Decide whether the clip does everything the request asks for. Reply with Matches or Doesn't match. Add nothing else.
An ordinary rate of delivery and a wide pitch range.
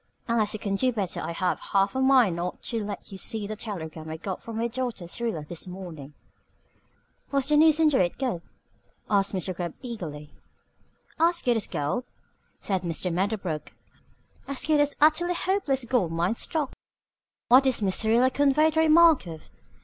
Matches